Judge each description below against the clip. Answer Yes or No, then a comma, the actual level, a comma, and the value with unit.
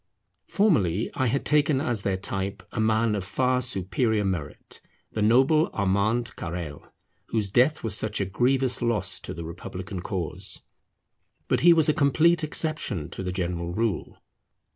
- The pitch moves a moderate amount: No, wide, 5.7 semitones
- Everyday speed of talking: Yes, average, 155 wpm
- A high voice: No, low, 110 Hz